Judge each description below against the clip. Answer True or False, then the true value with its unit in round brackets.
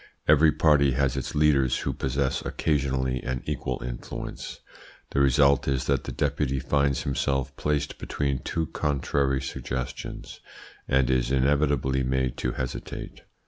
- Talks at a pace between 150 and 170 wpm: False (135 wpm)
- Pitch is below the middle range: True (70 Hz)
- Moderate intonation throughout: False (1.7 semitones)